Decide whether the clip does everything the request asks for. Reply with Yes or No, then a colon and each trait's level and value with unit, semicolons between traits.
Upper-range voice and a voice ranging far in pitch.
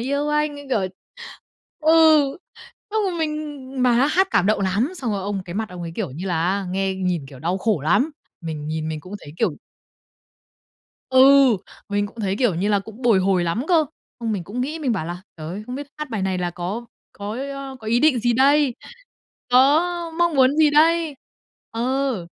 Yes: high, 230 Hz; wide, 7.3 semitones